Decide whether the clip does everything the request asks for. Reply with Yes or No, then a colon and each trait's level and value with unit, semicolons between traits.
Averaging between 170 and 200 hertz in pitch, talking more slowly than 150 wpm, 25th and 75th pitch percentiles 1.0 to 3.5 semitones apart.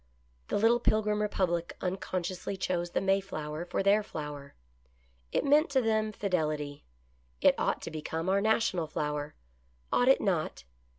No: medium, 185 Hz; average, 140 wpm; average, 5.1 semitones